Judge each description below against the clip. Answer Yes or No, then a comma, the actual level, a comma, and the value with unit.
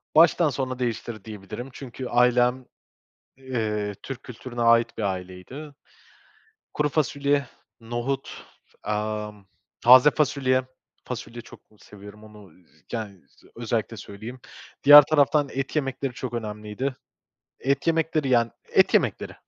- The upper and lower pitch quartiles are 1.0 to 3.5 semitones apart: No, average, 4.1 semitones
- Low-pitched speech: Yes, low, 125 Hz